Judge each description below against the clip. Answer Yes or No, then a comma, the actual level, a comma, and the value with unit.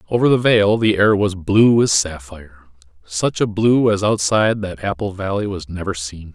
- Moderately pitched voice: No, very low, 95 Hz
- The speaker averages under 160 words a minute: No, average, 180 wpm